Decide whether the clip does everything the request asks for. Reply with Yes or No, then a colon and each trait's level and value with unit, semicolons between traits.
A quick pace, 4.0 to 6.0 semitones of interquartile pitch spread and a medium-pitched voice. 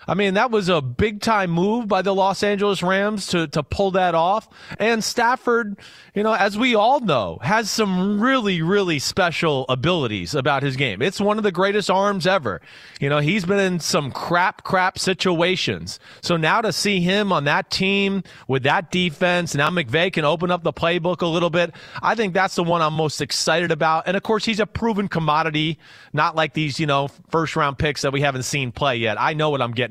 Yes: fast, 215 wpm; average, 4.6 semitones; medium, 180 Hz